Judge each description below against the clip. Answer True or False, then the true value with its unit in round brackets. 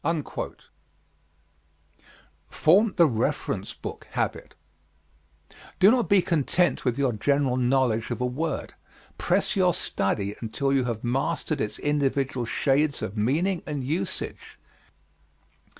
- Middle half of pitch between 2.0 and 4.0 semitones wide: False (4.7 semitones)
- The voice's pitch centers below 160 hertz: True (135 Hz)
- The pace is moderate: False (115 wpm)